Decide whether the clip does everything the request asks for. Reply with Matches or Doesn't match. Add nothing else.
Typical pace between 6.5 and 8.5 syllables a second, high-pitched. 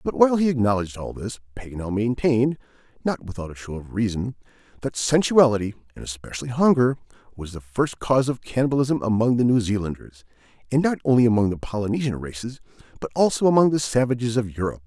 Doesn't match